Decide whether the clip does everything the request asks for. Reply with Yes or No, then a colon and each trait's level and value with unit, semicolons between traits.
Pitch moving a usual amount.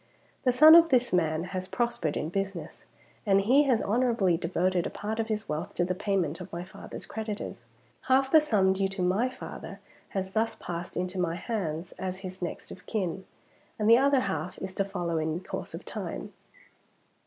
Yes: average, 4.1 semitones